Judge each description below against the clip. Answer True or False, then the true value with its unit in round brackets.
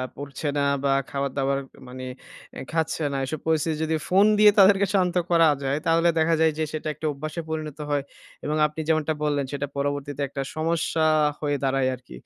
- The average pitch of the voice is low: False (150 Hz)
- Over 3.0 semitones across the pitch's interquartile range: False (2.5 semitones)